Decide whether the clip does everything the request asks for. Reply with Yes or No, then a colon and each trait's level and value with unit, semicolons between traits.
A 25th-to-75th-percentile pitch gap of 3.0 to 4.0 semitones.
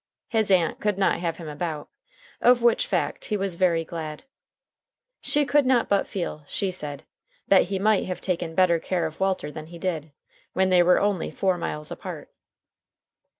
Yes: average, 3.3 semitones